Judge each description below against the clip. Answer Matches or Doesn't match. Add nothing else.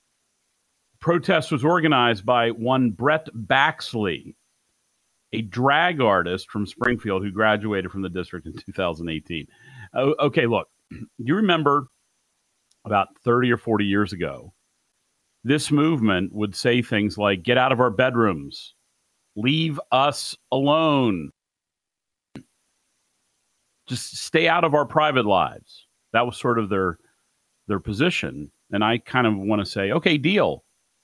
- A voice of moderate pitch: Doesn't match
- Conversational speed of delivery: Doesn't match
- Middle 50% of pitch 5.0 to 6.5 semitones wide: Matches